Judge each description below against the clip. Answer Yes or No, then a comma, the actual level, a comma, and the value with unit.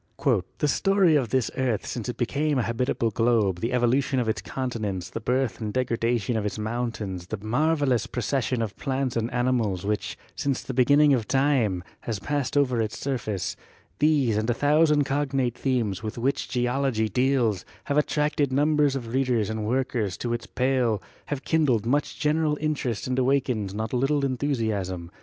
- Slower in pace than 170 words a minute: No, average, 175 wpm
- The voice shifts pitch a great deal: No, average, 3.9 semitones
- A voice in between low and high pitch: No, low, 125 Hz